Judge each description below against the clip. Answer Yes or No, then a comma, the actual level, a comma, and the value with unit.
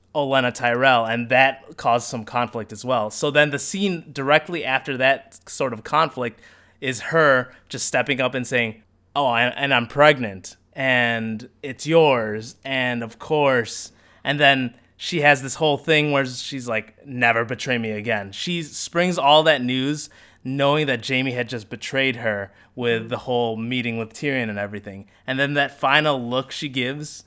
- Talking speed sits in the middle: Yes, average, 170 wpm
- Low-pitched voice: Yes, low, 130 Hz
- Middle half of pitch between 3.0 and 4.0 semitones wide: Yes, average, 3.6 semitones